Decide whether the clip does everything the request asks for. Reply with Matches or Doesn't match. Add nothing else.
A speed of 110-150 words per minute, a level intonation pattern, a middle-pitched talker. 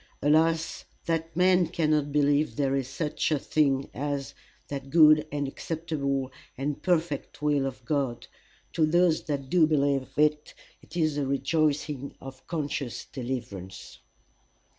Matches